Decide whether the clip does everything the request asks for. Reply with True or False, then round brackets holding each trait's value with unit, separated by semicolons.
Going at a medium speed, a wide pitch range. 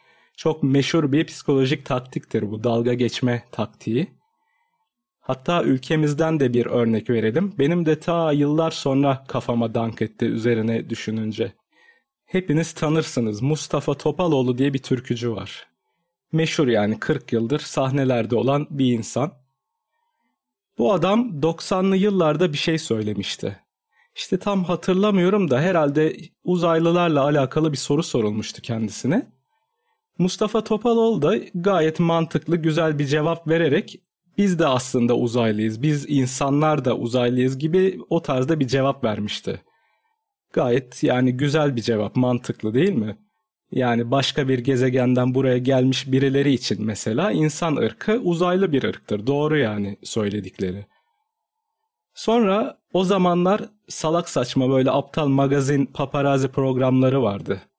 True (125 wpm; 5.7 semitones)